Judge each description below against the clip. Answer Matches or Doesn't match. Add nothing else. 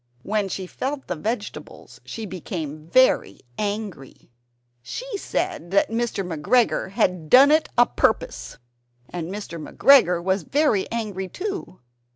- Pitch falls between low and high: Doesn't match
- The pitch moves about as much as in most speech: Doesn't match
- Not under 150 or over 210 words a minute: Doesn't match